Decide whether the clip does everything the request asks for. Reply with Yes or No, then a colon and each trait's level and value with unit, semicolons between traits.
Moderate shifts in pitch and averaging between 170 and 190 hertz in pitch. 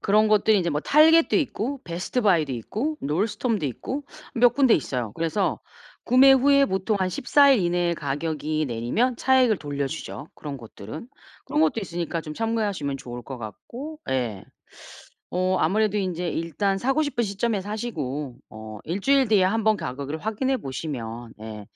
No: wide, 8.4 semitones; medium, 185 Hz